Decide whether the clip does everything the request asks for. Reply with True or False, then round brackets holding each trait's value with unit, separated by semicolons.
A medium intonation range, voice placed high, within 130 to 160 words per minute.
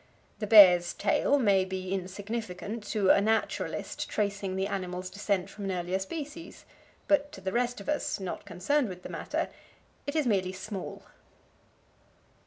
True (3.4 semitones; 200 Hz; 155 wpm)